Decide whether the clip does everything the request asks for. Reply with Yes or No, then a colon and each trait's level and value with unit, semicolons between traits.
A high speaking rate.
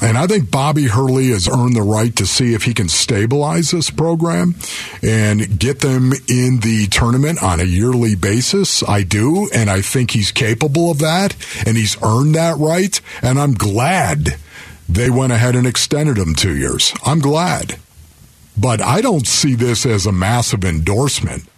No: average, 175 wpm